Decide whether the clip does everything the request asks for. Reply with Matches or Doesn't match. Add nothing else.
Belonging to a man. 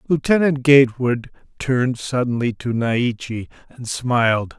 Matches